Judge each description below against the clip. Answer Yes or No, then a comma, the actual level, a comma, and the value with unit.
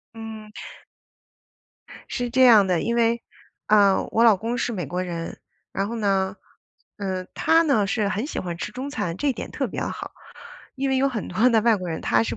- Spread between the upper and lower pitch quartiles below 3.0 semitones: No, average, 4.1 semitones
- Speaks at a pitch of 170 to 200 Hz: No, high, 215 Hz